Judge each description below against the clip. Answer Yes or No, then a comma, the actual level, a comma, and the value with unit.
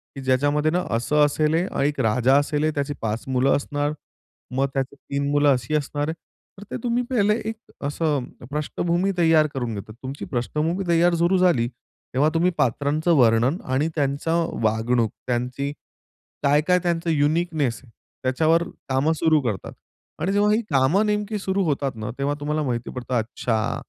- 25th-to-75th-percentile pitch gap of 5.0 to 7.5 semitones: No, average, 4.2 semitones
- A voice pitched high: No, medium, 145 Hz